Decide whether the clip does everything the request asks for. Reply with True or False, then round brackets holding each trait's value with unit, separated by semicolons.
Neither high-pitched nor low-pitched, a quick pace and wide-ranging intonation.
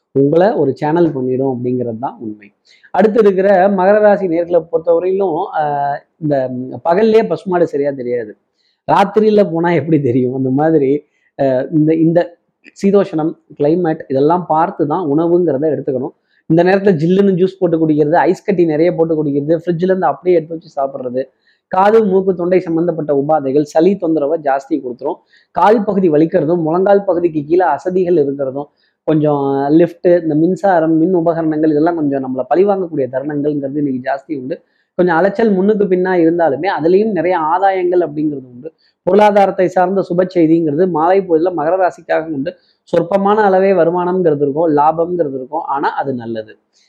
False (165 Hz; 135 wpm; 4.1 semitones)